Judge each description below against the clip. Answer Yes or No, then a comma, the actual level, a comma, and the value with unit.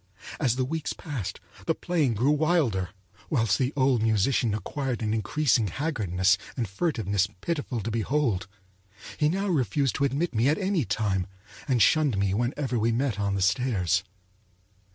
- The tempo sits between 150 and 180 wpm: Yes, average, 155 wpm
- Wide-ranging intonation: Yes, wide, 6.1 semitones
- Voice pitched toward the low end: Yes, low, 125 Hz